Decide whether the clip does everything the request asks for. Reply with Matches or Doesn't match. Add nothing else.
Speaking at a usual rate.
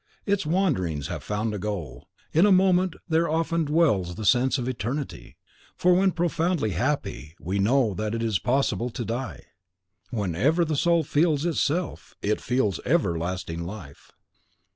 Matches